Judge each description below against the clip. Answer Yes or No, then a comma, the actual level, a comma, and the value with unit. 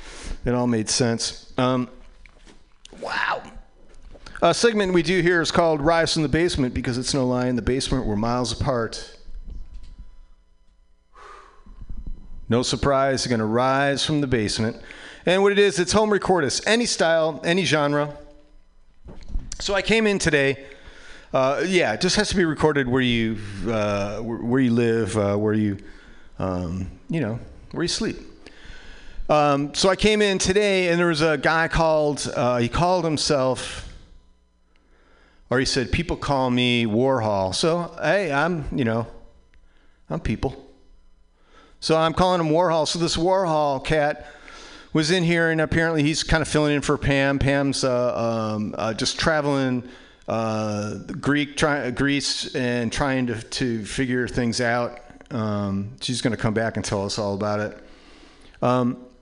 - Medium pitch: No, low, 130 Hz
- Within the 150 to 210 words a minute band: Yes, average, 160 wpm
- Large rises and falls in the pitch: Yes, wide, 6.0 semitones